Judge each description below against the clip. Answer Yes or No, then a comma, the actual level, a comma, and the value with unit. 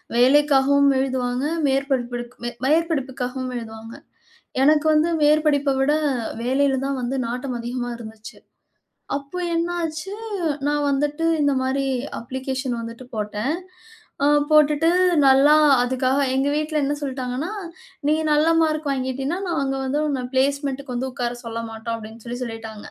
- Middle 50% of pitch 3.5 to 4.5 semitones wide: No, average, 3.0 semitones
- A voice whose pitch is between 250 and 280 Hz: Yes, very high, 270 Hz